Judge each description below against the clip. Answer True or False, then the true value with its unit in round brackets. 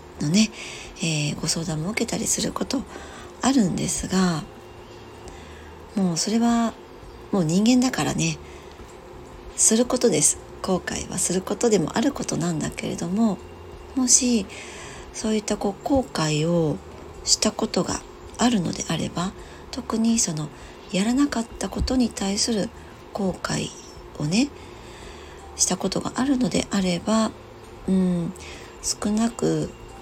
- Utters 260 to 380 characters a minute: False (245 characters per minute)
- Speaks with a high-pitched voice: True (205 Hz)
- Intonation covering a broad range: False (5.0 semitones)